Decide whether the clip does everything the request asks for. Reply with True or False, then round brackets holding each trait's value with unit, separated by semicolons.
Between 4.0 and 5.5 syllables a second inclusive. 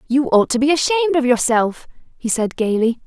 True (5.4 syllables/s)